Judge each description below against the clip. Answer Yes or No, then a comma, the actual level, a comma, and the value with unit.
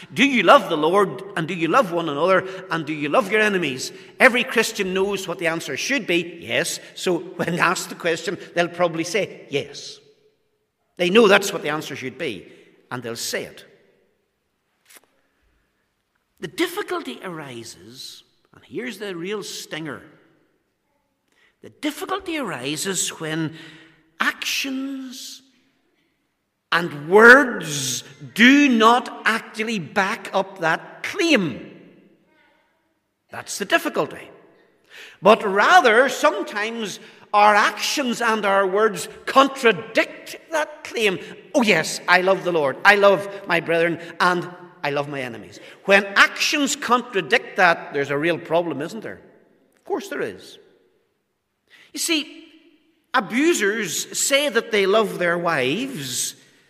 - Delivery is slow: Yes, slow, 130 wpm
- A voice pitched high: Yes, high, 200 Hz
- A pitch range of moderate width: No, wide, 8.4 semitones